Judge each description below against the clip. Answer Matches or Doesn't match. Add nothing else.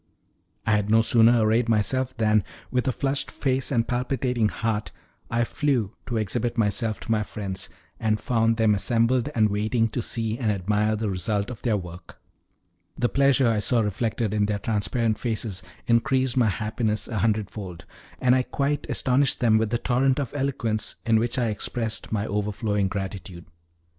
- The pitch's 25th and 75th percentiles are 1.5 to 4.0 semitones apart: Matches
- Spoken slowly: Doesn't match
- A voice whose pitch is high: Doesn't match